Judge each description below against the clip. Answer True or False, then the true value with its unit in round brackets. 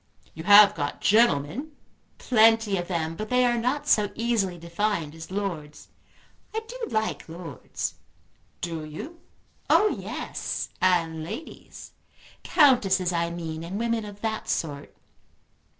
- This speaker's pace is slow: True (130 wpm)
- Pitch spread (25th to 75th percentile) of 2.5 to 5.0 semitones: False (5.5 semitones)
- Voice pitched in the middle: False (195 Hz)